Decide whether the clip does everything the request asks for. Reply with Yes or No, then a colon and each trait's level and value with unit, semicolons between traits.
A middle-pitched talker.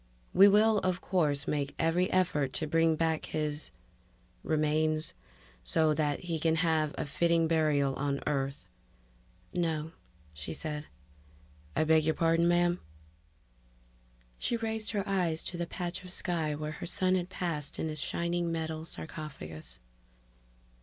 Yes: medium, 160 Hz